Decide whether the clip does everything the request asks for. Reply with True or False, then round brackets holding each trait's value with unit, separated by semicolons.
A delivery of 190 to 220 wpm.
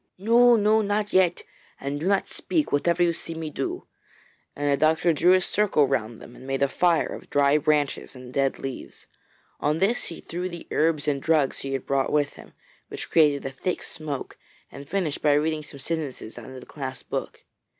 True (200 wpm)